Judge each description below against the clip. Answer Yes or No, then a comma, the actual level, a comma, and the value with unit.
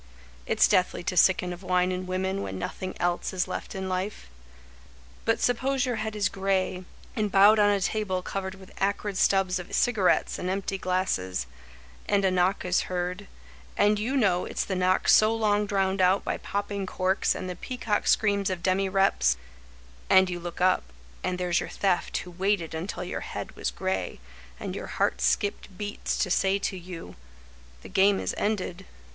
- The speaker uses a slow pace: No, average, 180 wpm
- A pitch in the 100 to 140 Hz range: No, high, 190 Hz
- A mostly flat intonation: Yes, narrow, 1.9 semitones